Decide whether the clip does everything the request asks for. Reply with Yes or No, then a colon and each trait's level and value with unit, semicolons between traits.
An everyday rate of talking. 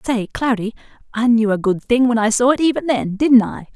No: fast, 240 wpm